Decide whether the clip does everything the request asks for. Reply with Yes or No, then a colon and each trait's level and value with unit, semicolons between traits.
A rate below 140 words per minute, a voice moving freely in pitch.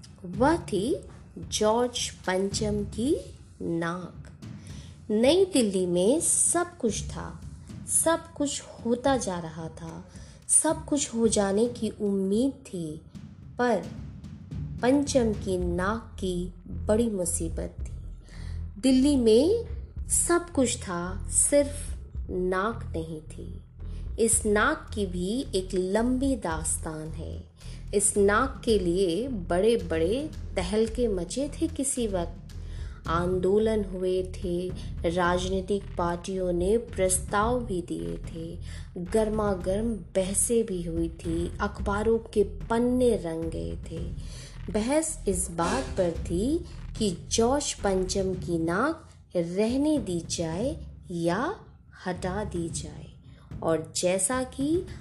Yes: slow, 110 wpm; wide, 5.7 semitones